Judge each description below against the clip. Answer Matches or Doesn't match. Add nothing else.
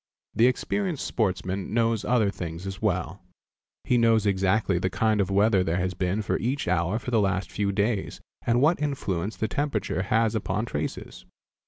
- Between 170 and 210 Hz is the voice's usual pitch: Doesn't match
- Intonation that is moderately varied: Matches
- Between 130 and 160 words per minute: Doesn't match